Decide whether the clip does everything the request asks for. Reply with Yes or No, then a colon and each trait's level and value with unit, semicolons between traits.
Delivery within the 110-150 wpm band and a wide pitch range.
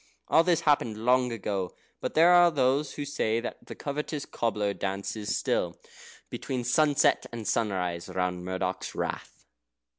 Yes: average, 145 wpm; wide, 6.6 semitones